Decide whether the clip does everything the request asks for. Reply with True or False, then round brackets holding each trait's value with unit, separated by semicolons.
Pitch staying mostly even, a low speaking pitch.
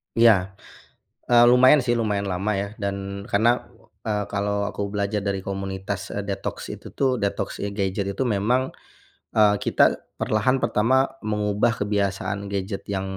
True (2.1 semitones; 100 Hz)